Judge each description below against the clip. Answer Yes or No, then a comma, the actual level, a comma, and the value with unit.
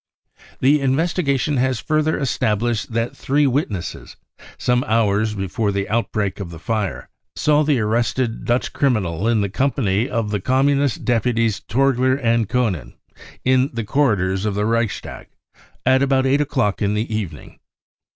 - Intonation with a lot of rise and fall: No, average, 4.2 semitones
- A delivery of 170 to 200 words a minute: No, average, 155 wpm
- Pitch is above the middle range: No, low, 115 Hz